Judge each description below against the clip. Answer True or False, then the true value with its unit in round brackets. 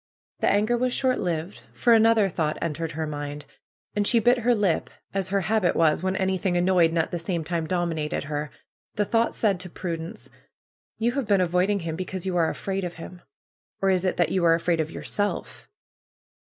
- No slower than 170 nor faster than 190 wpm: False (205 wpm)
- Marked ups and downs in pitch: False (3.7 semitones)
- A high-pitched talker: False (180 Hz)